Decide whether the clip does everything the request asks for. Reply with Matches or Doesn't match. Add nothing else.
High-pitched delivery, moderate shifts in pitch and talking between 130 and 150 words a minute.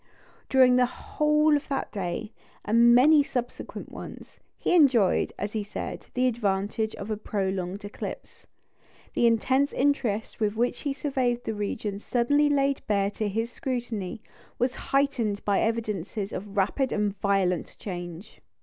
Matches